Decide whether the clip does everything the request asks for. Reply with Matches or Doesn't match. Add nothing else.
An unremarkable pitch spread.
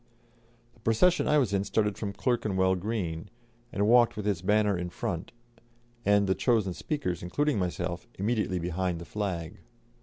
Matches